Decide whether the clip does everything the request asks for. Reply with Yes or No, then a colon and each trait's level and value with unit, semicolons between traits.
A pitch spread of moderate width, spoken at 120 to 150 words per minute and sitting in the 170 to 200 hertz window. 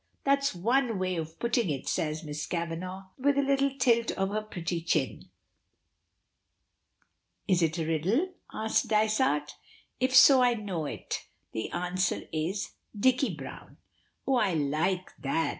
No: wide, 6.9 semitones; average, 140 wpm; high, 190 Hz